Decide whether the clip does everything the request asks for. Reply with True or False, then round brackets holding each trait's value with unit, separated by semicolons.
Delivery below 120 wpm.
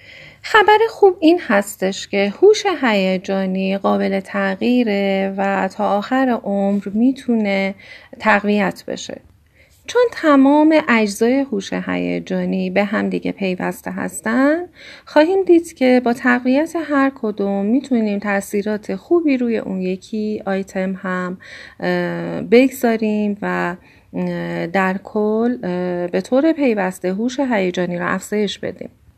True (110 wpm)